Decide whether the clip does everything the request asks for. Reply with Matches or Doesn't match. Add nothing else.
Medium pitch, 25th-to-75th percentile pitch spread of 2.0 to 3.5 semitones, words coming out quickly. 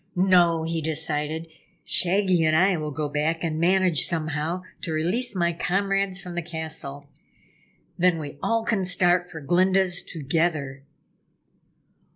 Doesn't match